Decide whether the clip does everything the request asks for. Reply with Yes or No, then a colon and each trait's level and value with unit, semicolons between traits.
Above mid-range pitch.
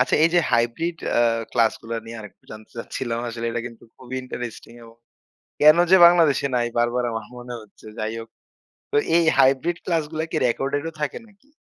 No: low, 125 Hz